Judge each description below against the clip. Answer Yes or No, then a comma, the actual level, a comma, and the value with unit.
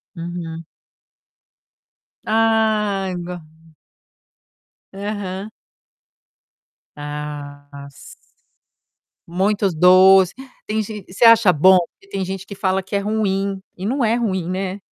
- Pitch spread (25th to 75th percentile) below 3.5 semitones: Yes, average, 2.8 semitones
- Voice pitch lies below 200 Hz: Yes, high, 190 Hz